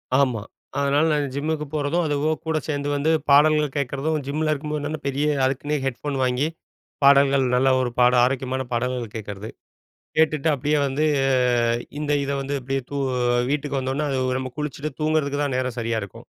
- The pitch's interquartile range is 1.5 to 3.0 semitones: Yes, narrow, 2.4 semitones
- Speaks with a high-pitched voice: No, medium, 140 Hz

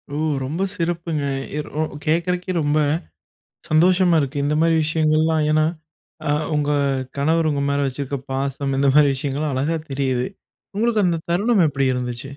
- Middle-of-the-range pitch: Yes, medium, 150 Hz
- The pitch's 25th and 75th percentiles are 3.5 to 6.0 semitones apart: No, average, 3.1 semitones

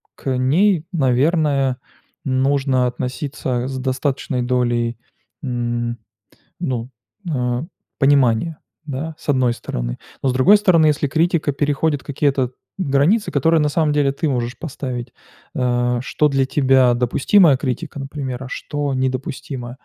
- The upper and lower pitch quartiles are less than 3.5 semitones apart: Yes, average, 2.9 semitones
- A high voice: No, low, 135 Hz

